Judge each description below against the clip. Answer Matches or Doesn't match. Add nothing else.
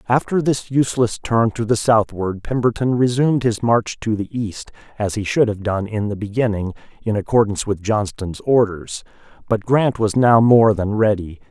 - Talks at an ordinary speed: Matches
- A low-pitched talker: Matches